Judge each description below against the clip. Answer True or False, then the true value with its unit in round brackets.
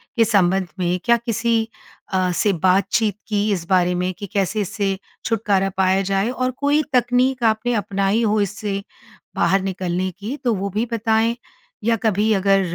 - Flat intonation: False (3.1 semitones)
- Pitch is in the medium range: False (205 Hz)